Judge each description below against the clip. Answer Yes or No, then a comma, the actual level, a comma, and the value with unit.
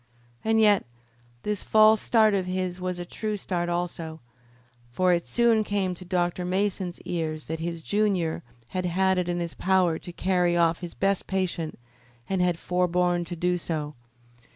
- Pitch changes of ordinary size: No, narrow, 1.8 semitones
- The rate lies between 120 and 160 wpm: No, average, 170 wpm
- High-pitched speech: No, medium, 180 Hz